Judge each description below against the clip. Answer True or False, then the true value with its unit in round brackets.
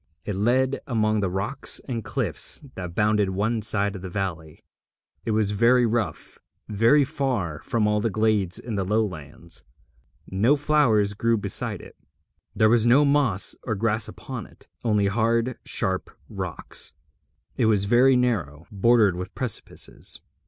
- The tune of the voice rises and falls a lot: False (3.4 semitones)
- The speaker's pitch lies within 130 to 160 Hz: False (110 Hz)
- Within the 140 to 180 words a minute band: True (150 wpm)